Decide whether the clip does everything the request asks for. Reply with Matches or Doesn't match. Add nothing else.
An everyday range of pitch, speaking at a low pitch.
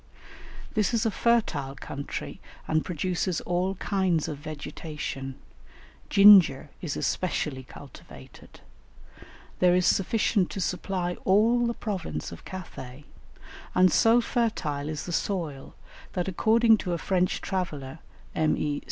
Doesn't match